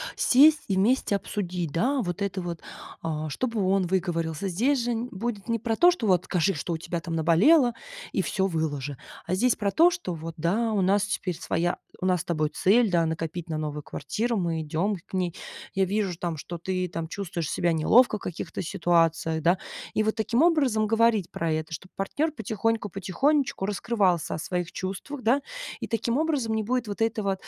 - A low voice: No, high, 190 Hz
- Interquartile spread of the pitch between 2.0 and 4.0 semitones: No, average, 5.2 semitones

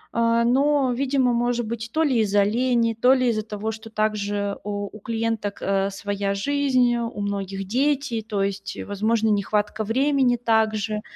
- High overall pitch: Yes, high, 225 Hz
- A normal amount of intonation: Yes, average, 3.1 semitones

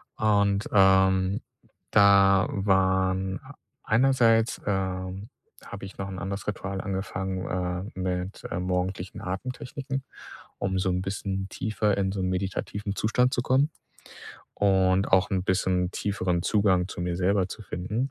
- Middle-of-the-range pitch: No, very low, 95 Hz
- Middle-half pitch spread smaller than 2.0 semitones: Yes, narrow, 1.6 semitones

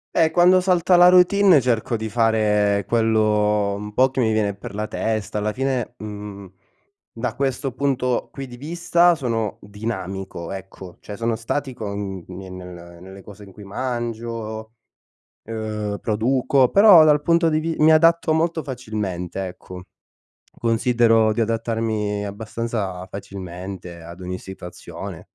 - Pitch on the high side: No, low, 110 Hz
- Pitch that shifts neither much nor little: Yes, average, 4.6 semitones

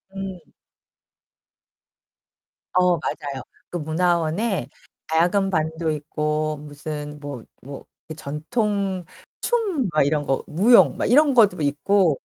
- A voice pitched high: No, medium, 160 Hz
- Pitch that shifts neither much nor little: Yes, average, 4.5 semitones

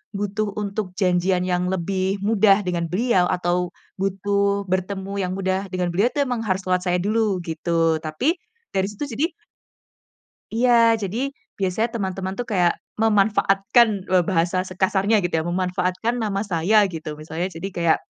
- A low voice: No, high, 190 Hz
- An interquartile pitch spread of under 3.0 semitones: Yes, narrow, 2.5 semitones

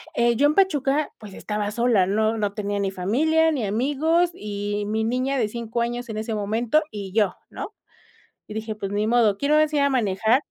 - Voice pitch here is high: Yes, high, 225 Hz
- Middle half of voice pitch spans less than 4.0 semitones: No, average, 4.7 semitones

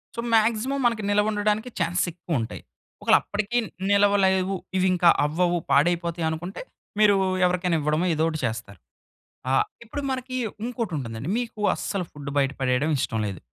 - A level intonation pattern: No, wide, 5.6 semitones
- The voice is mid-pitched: Yes, medium, 180 Hz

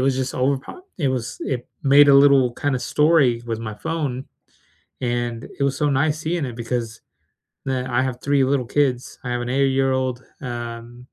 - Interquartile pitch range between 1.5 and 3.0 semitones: Yes, narrow, 2.5 semitones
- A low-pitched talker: Yes, low, 130 Hz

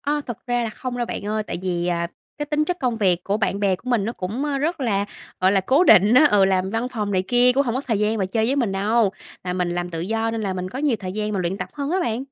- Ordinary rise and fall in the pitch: Yes, average, 4.7 semitones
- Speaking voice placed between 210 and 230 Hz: Yes, high, 220 Hz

